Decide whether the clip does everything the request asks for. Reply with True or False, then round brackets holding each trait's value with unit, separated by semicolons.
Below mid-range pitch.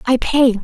False (250 Hz)